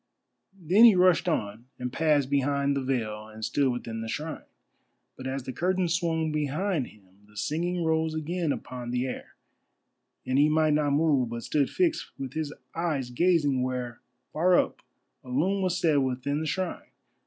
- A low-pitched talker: No, medium, 145 Hz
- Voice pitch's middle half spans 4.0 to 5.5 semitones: Yes, average, 4.6 semitones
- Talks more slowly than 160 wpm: No, average, 175 wpm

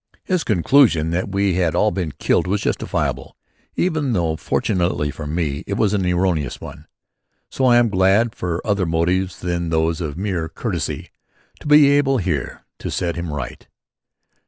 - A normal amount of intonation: Yes, average, 4.2 semitones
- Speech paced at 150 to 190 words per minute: Yes, average, 165 wpm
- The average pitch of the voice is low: Yes, very low, 90 Hz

